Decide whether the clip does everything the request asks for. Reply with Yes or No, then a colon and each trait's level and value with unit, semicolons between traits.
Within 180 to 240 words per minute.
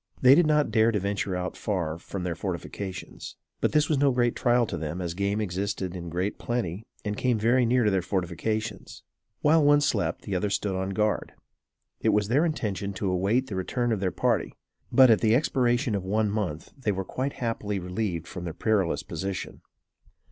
Yes: average, 195 wpm